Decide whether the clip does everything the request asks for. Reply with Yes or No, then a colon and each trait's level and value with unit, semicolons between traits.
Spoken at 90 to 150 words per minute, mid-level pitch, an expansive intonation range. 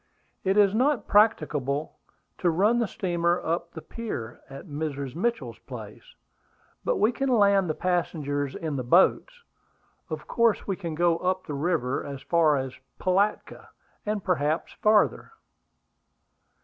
Yes: average, 145 wpm; medium, 175 Hz; wide, 5.8 semitones